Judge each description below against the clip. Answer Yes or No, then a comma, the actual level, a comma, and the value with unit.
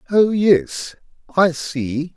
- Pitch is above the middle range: No, medium, 165 Hz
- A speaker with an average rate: No, slow, 110 wpm